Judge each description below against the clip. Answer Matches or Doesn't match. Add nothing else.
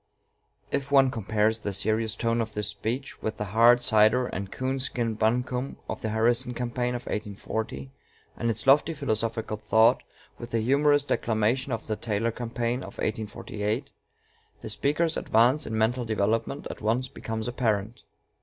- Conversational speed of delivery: Matches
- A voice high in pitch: Doesn't match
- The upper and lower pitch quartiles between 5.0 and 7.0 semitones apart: Doesn't match